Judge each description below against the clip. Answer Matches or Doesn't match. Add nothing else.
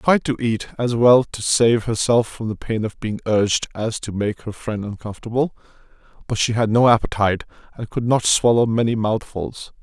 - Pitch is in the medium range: Doesn't match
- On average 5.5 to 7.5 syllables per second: Doesn't match